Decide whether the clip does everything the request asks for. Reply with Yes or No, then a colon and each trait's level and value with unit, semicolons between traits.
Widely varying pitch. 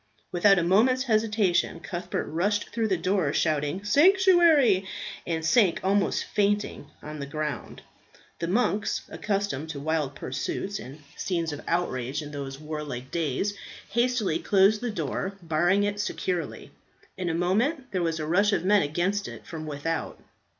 No: average, 4.9 semitones